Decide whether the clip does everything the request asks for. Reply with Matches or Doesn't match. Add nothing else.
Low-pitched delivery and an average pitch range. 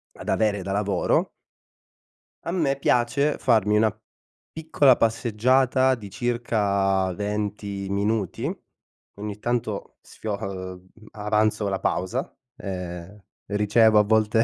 Matches